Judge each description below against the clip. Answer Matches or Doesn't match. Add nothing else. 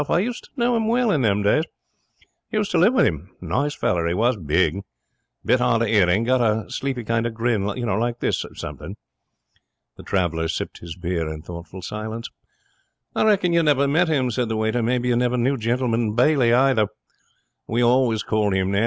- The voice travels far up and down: Doesn't match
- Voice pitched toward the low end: Matches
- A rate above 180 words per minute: Matches